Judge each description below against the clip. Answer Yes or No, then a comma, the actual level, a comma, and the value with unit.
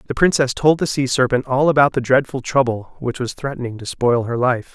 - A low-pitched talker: Yes, low, 130 Hz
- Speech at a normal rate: No, fast, 230 wpm